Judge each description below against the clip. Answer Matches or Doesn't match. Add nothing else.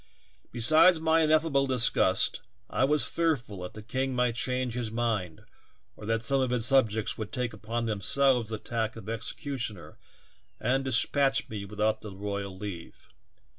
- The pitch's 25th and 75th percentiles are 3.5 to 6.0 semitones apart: Matches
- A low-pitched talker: Matches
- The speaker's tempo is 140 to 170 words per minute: Matches